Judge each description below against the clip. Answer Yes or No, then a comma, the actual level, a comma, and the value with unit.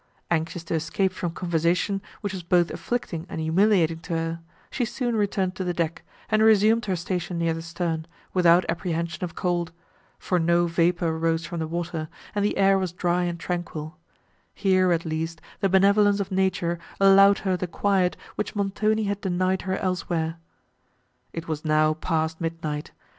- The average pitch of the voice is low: No, medium, 175 Hz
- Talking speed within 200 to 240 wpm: No, average, 170 wpm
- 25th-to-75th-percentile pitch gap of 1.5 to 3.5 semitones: Yes, average, 2.7 semitones